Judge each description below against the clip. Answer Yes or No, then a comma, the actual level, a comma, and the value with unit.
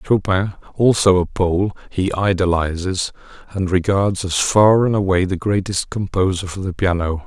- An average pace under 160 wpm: Yes, average, 150 wpm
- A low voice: Yes, very low, 95 Hz